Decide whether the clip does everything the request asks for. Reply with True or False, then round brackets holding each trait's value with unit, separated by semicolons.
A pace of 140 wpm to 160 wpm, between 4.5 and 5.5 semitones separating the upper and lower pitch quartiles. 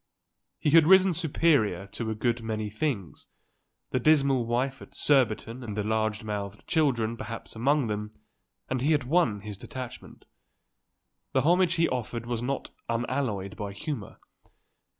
True (150 wpm; 4.8 semitones)